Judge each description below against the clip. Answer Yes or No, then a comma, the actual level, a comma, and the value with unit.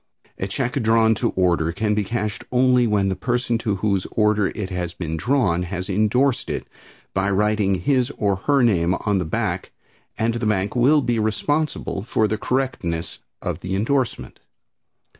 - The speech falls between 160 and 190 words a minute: Yes, average, 170 wpm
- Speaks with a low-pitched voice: Yes, low, 105 Hz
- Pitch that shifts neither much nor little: Yes, average, 4.1 semitones